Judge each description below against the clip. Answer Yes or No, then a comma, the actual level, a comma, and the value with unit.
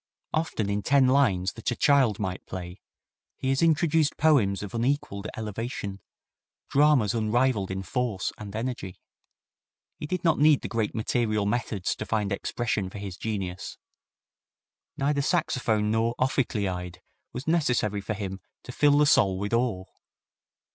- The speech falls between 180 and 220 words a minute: No, average, 145 wpm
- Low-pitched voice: Yes, low, 110 Hz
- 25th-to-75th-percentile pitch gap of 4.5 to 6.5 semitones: Yes, average, 5.3 semitones